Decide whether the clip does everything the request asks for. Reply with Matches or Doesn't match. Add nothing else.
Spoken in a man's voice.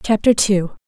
Doesn't match